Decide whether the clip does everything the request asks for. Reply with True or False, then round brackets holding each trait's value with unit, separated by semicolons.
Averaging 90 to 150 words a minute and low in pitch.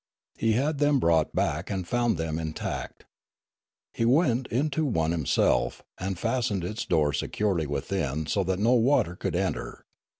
False (160 wpm; 95 Hz)